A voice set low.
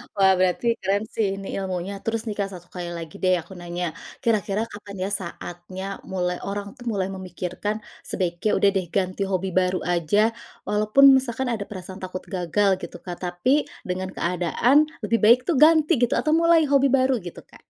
No: high, 195 Hz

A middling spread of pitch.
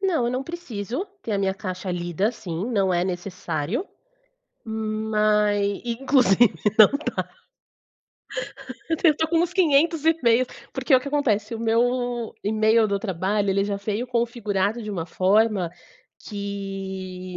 Yes: average, 4.0 semitones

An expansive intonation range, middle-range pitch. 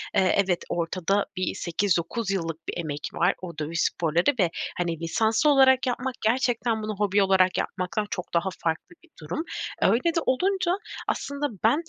No: wide, 6.4 semitones; high, 195 Hz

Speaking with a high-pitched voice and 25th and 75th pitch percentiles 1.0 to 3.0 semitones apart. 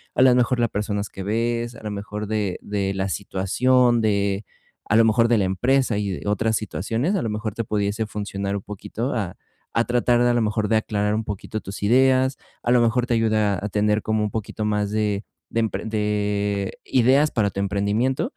No: low, 105 Hz; narrow, 2.5 semitones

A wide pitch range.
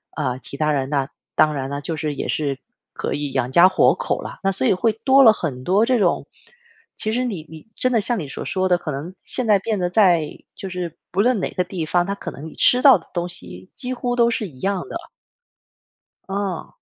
Yes: wide, 6.5 semitones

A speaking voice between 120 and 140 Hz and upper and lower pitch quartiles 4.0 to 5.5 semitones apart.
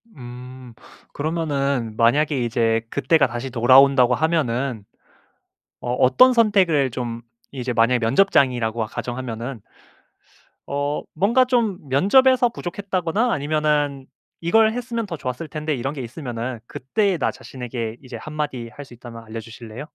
Yes: low, 135 Hz; average, 5.2 semitones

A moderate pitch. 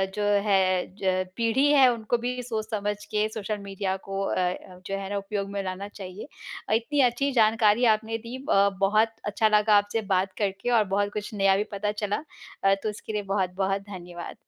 No: high, 205 Hz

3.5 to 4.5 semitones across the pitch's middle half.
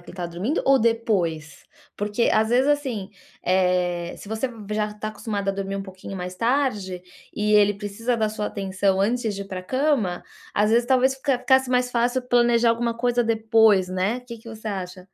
Yes: average, 3.9 semitones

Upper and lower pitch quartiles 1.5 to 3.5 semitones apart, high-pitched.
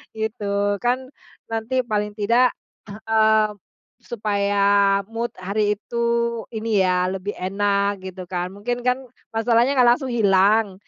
Yes: narrow, 2.4 semitones; high, 210 Hz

